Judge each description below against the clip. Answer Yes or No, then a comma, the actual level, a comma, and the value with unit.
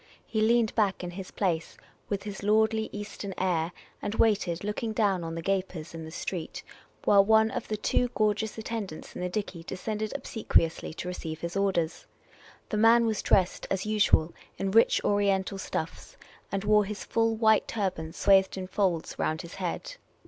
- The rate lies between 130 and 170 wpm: No, average, 180 wpm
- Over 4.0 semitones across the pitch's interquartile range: No, average, 3.2 semitones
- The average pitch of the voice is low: No, high, 195 Hz